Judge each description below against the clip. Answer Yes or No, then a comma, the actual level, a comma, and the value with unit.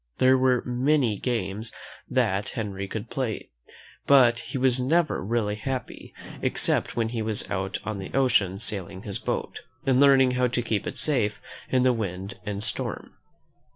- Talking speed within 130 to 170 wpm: Yes, average, 160 wpm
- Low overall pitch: Yes, low, 115 Hz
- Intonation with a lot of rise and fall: No, average, 4.0 semitones